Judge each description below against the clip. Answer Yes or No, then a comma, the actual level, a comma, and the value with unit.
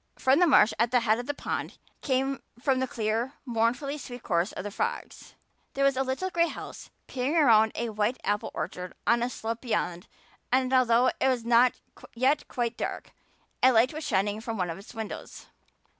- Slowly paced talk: No, average, 190 wpm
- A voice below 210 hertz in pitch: No, high, 245 Hz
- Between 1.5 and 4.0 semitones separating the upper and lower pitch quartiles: Yes, average, 3.0 semitones